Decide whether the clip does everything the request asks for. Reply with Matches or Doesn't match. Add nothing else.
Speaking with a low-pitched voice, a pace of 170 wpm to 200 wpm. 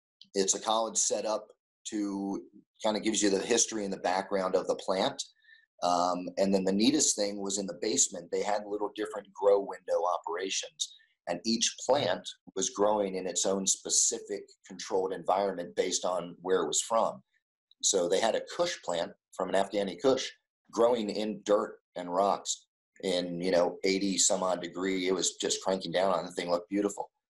Matches